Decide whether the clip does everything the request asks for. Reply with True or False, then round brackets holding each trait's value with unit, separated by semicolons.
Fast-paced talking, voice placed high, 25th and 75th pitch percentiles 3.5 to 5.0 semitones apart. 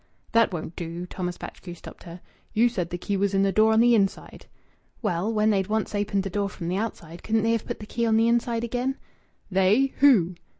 True (225 wpm; 205 Hz; 3.9 semitones)